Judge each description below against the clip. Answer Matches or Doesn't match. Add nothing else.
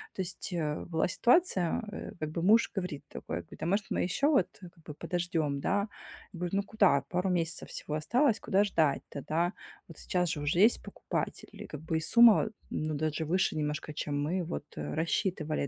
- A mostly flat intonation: Doesn't match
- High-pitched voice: Doesn't match